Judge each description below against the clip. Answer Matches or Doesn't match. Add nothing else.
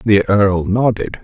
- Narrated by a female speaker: Doesn't match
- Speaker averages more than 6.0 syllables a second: Doesn't match